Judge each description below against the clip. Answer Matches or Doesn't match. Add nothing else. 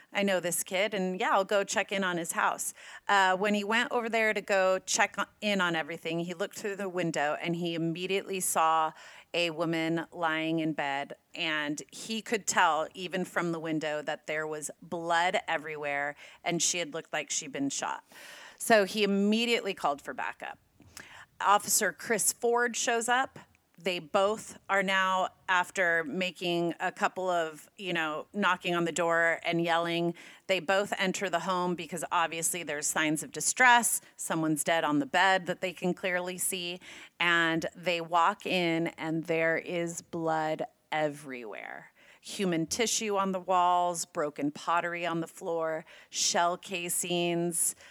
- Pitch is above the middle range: Doesn't match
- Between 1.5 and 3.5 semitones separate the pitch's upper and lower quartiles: Matches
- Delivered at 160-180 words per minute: Matches